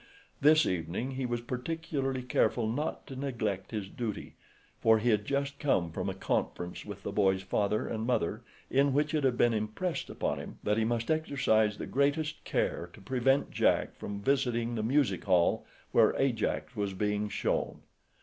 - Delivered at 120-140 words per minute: No, average, 170 wpm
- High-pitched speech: No, low, 120 Hz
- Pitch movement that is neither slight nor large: Yes, average, 4.7 semitones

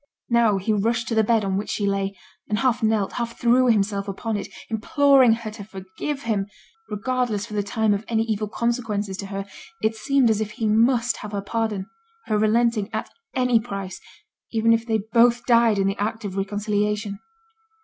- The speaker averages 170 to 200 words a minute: Yes, average, 190 wpm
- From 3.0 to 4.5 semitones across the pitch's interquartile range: No, narrow, 2.4 semitones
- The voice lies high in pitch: Yes, high, 220 Hz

